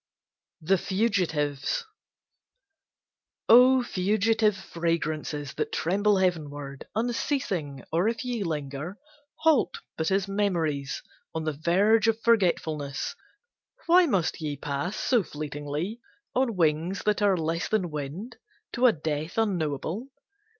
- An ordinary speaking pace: No, slow, 115 wpm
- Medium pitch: Yes, medium, 180 Hz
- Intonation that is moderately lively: No, wide, 6.1 semitones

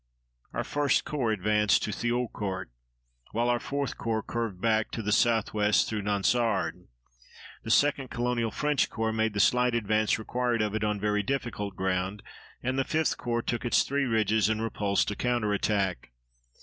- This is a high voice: No, low, 110 Hz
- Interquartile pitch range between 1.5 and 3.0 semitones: Yes, average, 2.7 semitones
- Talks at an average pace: Yes, average, 160 wpm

